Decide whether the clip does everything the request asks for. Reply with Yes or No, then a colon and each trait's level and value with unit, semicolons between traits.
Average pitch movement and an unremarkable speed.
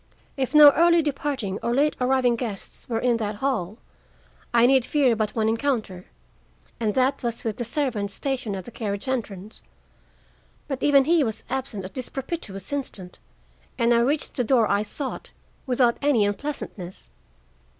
Yes: average, 4.4 semitones; average, 160 wpm